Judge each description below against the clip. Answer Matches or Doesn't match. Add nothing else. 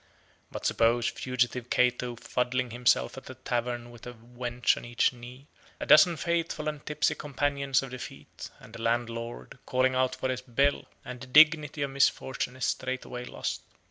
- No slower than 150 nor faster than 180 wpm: Matches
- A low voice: Matches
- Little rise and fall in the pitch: Matches